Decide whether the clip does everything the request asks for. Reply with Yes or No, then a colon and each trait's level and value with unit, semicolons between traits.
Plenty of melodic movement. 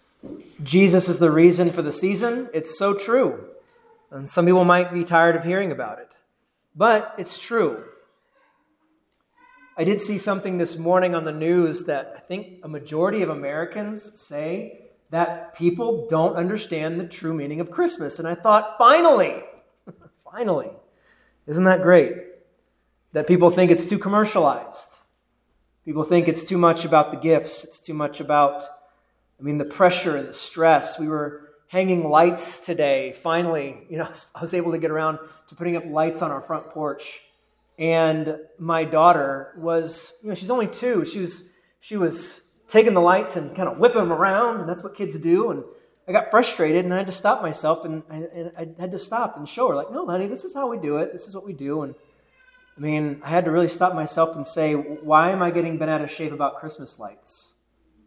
No: average, 3.7 semitones